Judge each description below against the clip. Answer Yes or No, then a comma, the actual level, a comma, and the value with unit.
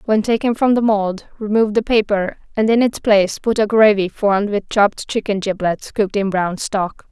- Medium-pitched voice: No, high, 210 Hz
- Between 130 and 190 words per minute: No, average, 200 wpm